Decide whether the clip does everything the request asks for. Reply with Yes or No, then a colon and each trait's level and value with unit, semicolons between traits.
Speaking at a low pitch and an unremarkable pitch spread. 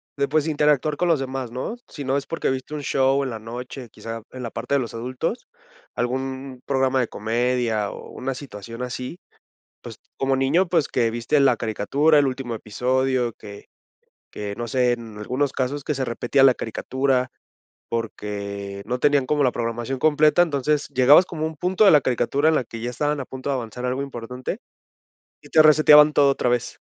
Yes: low, 130 Hz; average, 3.3 semitones